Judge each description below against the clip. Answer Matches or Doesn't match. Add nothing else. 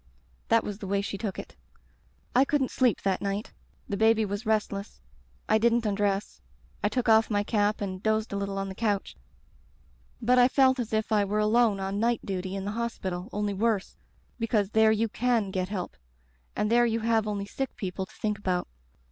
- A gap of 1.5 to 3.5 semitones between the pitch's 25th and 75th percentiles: Matches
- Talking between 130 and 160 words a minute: Doesn't match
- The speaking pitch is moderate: Doesn't match